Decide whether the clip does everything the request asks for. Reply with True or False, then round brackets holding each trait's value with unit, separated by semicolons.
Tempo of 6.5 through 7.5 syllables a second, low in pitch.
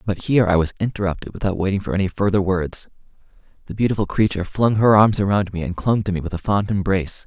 True (6.7 syllables/s; 95 Hz)